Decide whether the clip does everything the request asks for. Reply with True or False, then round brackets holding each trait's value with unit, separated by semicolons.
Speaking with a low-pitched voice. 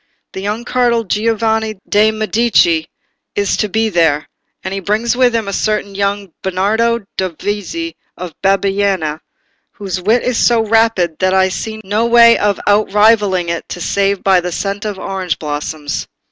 False (205 Hz)